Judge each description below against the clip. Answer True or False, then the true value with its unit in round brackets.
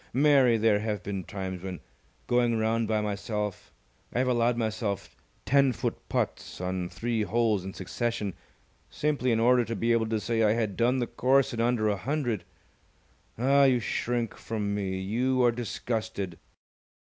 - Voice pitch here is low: True (115 Hz)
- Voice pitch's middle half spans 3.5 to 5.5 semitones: False (2.9 semitones)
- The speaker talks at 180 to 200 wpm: False (165 wpm)